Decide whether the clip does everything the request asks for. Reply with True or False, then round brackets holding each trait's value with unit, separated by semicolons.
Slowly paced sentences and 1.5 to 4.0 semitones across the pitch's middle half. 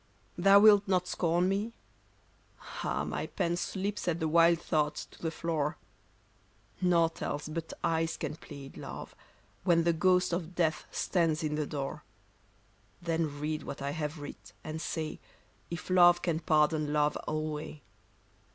False (150 wpm; 2.4 semitones)